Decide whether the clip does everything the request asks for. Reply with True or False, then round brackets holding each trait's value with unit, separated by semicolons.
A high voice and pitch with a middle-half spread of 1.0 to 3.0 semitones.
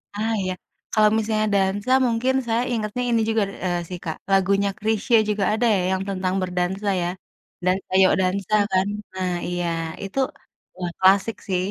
True (195 Hz; 2.7 semitones)